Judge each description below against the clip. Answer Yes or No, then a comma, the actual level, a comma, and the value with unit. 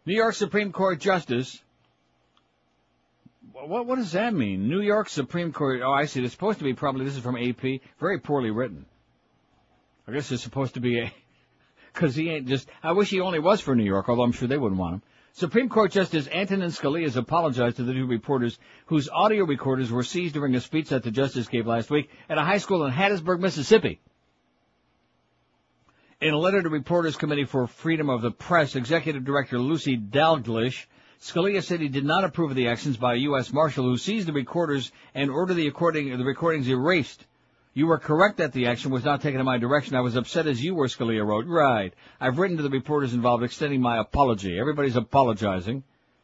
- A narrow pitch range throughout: No, average, 5.2 semitones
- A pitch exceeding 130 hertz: Yes, medium, 140 Hz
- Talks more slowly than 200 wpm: No, fast, 205 wpm